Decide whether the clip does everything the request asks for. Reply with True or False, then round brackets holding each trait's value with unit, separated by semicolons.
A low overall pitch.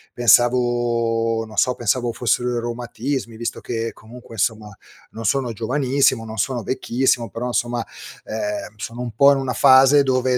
True (120 Hz)